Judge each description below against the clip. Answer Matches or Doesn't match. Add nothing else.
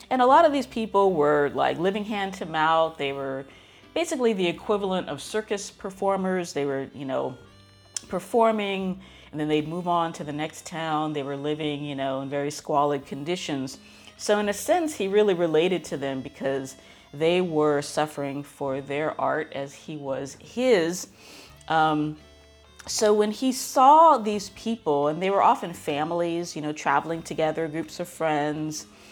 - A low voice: Doesn't match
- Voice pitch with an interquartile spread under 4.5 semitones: Doesn't match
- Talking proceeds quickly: Doesn't match